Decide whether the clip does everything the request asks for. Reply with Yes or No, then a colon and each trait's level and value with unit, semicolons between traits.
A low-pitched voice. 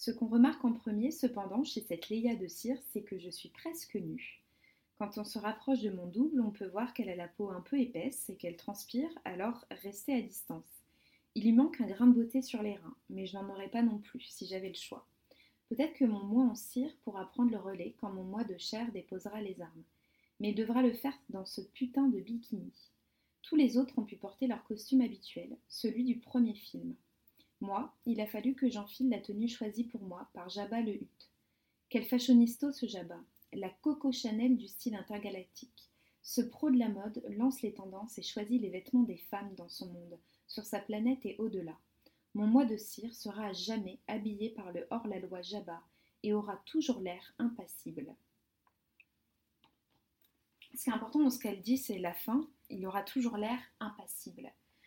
No: high, 220 Hz